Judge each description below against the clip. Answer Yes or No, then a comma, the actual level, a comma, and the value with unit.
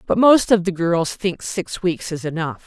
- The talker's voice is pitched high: No, medium, 180 Hz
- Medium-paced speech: No, fast, 225 wpm